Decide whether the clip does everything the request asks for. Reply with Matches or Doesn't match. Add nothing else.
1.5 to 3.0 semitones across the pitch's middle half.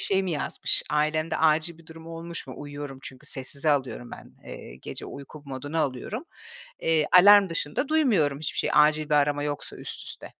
Matches